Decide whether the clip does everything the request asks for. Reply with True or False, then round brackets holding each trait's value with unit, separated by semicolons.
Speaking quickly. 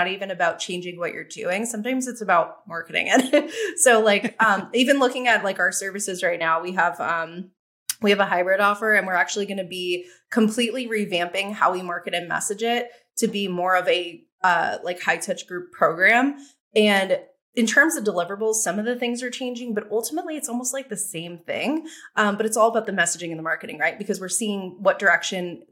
True (210 wpm)